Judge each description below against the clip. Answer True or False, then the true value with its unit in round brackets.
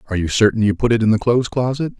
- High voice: False (115 Hz)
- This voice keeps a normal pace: False (300 wpm)